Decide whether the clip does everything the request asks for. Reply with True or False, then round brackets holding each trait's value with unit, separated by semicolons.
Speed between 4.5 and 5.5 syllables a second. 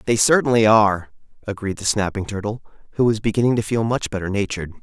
False (6.7 syllables/s)